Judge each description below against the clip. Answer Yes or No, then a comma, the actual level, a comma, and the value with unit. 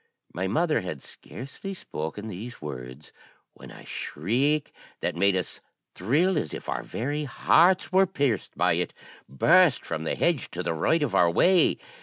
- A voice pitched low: Yes, low, 115 Hz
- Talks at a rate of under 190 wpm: Yes, average, 165 wpm